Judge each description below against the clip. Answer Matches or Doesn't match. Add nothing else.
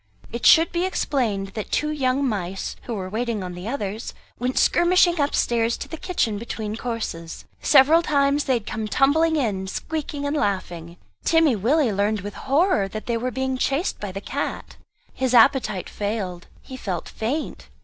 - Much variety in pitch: Matches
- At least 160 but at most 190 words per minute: Matches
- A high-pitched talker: Matches